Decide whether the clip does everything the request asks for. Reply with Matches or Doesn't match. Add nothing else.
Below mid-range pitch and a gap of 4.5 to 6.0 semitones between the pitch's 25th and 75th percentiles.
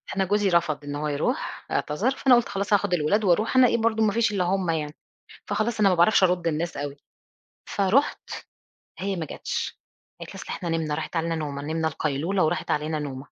Doesn't match